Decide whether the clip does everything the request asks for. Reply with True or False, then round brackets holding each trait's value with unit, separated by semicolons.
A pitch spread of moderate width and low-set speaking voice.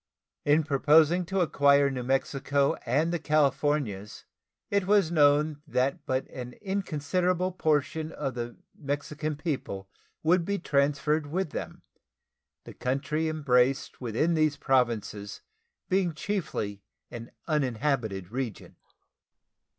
False (3.6 semitones; 145 Hz)